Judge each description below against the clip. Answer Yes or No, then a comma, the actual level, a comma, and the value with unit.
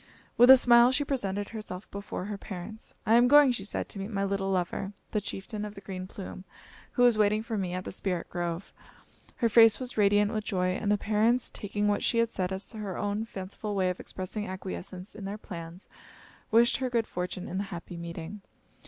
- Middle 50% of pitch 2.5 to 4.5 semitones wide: Yes, average, 3.0 semitones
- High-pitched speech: Yes, high, 205 Hz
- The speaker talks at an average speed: No, fast, 215 wpm